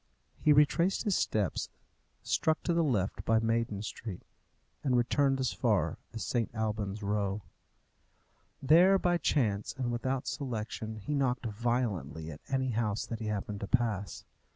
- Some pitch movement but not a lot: Yes, average, 4.3 semitones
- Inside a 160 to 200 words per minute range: No, average, 150 wpm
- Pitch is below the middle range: Yes, low, 115 Hz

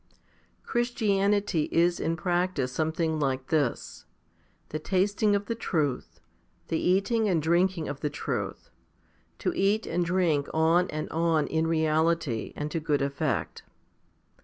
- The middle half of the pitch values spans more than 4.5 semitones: No, average, 3.7 semitones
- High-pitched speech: No, medium, 165 Hz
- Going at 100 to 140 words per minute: Yes, slow, 135 wpm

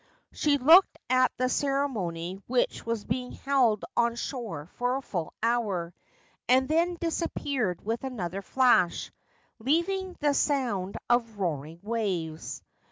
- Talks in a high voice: Yes, high, 240 Hz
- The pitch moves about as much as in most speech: No, wide, 6.1 semitones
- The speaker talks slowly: Yes, slow, 125 wpm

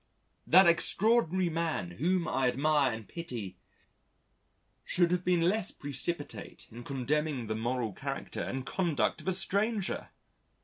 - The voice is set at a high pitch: No, medium, 155 Hz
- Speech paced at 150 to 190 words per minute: No, slow, 135 wpm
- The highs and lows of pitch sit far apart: Yes, wide, 6.3 semitones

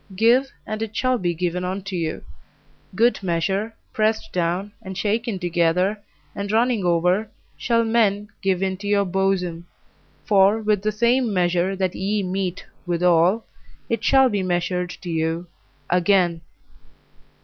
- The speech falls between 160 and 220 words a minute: No, average, 140 wpm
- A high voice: Yes, high, 195 Hz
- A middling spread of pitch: Yes, average, 3.3 semitones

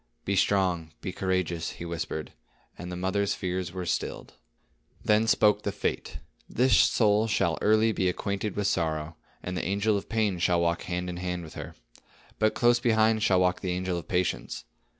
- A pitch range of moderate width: Yes, average, 3.0 semitones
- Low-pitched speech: Yes, very low, 95 Hz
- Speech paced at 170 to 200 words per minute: Yes, average, 180 wpm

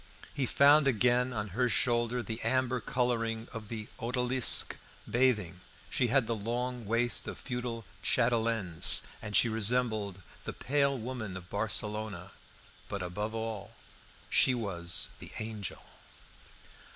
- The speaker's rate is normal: No, slow, 125 wpm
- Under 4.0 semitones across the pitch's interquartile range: Yes, average, 3.0 semitones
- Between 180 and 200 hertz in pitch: No, low, 115 Hz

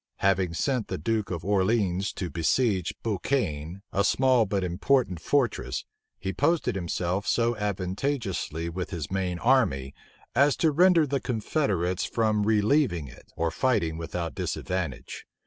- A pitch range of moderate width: No, wide, 5.8 semitones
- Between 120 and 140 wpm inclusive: Yes, slow, 135 wpm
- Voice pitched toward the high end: No, low, 100 Hz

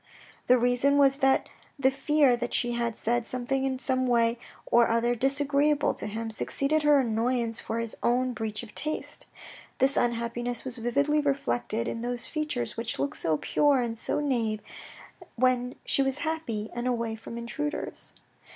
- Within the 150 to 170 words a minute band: Yes, average, 165 wpm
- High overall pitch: Yes, high, 245 Hz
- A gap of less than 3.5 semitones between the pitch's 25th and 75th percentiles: Yes, average, 2.9 semitones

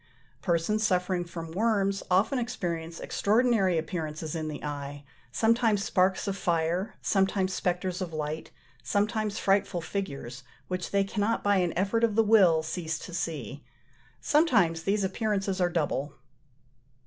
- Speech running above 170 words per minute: No, slow, 135 wpm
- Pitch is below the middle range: No, medium, 185 Hz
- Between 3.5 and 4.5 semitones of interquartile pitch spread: Yes, average, 3.8 semitones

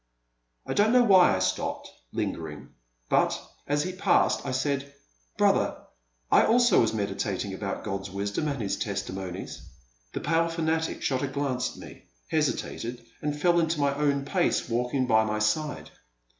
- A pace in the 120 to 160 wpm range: Yes, average, 155 wpm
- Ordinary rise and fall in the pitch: No, wide, 7.0 semitones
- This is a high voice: No, low, 135 Hz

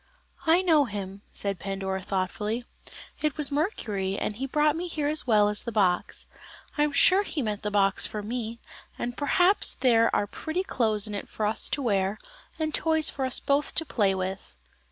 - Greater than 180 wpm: Yes, average, 195 wpm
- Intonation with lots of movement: Yes, wide, 6.7 semitones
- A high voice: Yes, high, 230 Hz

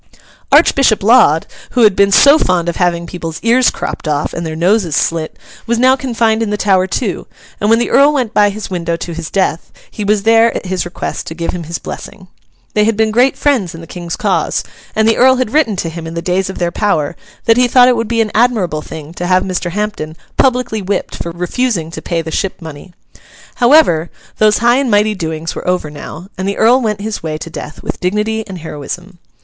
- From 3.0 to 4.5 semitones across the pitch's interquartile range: No, average, 5.1 semitones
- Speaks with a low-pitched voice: No, high, 195 Hz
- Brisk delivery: Yes, fast, 225 wpm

